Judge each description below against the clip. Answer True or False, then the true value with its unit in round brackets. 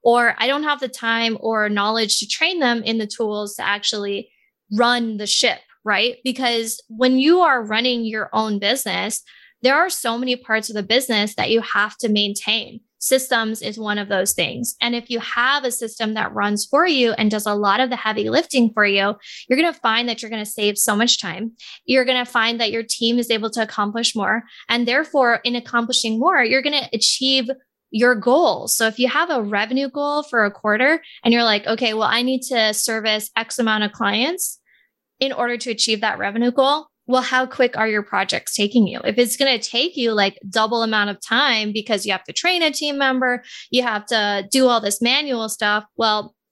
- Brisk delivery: True (210 wpm)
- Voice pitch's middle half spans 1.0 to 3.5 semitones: True (3.0 semitones)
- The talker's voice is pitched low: False (230 Hz)